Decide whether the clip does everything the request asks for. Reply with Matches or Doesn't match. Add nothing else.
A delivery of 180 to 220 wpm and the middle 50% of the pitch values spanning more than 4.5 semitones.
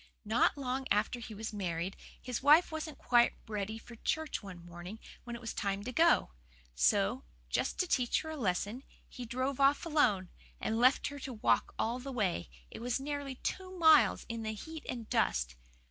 Matches